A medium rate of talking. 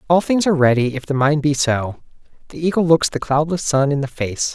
No: fast, 235 wpm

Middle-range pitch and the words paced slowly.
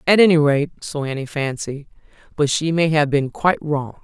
No: medium, 150 Hz; average, 195 wpm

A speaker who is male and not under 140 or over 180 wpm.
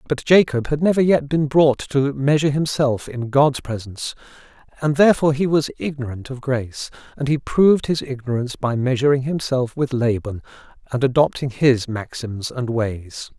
Yes: male; average, 160 wpm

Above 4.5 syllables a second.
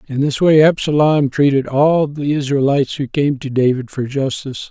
Yes: 5.1 syllables/s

